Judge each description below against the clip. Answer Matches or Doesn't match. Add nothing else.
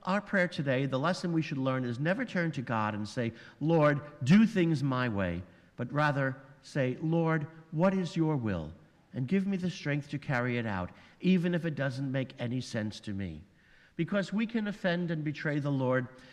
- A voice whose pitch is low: Doesn't match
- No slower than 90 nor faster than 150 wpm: Doesn't match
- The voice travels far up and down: Matches